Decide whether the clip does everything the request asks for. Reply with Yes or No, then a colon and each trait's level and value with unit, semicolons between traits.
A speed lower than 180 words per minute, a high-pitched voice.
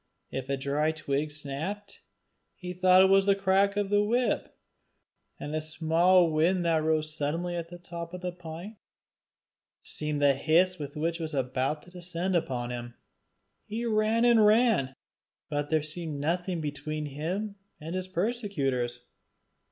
No: average, 160 wpm; medium, 165 Hz